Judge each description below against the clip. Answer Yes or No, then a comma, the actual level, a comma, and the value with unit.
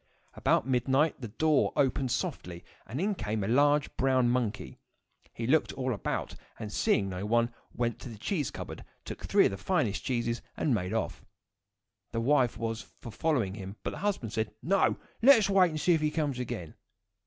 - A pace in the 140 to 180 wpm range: No, average, 195 wpm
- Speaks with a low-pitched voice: Yes, low, 125 Hz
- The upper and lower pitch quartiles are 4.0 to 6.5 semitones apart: Yes, average, 5.2 semitones